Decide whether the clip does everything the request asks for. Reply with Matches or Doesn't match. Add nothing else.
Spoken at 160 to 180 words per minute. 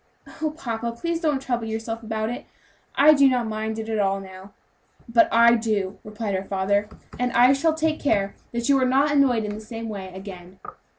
Doesn't match